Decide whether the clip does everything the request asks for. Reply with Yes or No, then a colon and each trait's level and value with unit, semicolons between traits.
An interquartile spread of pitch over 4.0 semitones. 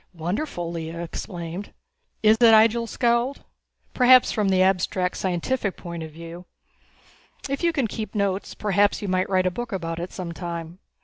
Yes: average, 4.6 semitones